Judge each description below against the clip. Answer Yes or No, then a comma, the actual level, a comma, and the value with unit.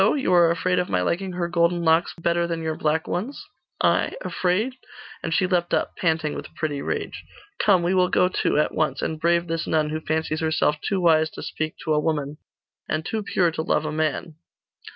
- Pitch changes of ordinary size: No, narrow, 2.2 semitones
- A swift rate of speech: Yes, fast, 210 wpm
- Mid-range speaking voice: Yes, medium, 165 Hz